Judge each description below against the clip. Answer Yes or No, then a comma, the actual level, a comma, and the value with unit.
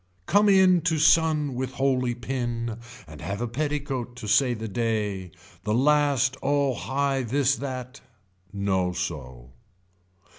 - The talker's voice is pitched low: Yes, low, 125 Hz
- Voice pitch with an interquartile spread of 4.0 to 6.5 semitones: Yes, average, 4.5 semitones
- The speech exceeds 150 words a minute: No, slow, 135 wpm